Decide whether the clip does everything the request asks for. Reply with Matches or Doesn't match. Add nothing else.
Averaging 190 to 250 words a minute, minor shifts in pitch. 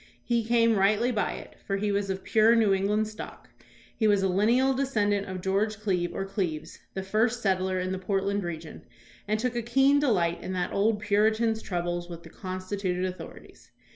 Doesn't match